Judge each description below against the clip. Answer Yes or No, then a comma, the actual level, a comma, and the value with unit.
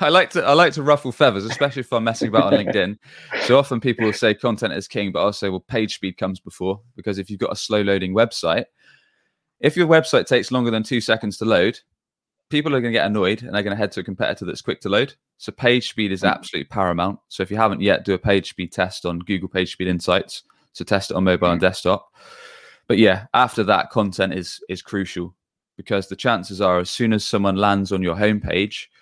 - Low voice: Yes, low, 100 Hz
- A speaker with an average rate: No, fast, 240 wpm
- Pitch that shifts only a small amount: No, average, 3.8 semitones